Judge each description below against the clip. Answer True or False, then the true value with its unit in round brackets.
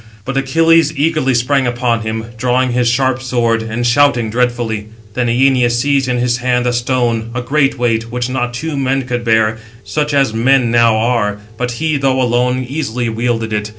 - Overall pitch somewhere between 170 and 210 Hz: False (125 Hz)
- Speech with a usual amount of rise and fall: False (2.3 semitones)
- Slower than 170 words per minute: False (185 wpm)